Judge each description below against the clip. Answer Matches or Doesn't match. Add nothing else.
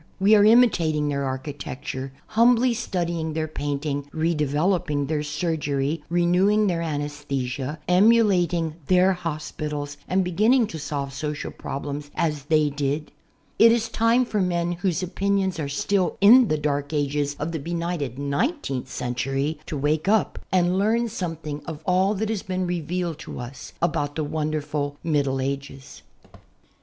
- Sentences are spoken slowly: Doesn't match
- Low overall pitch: Doesn't match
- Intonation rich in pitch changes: Doesn't match